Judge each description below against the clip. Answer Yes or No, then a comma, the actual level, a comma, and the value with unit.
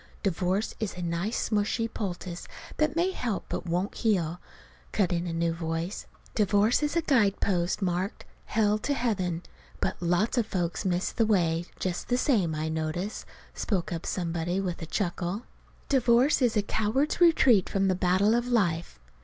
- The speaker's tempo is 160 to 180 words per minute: Yes, average, 165 wpm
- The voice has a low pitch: No, high, 195 Hz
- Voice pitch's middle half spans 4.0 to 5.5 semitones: Yes, average, 4.5 semitones